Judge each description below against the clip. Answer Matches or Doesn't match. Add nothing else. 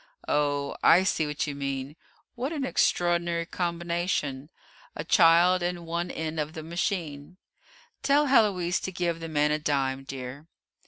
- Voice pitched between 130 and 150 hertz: Doesn't match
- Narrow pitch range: Doesn't match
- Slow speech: Doesn't match